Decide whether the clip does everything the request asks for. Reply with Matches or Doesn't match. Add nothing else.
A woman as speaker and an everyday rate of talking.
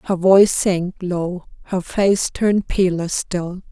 Matches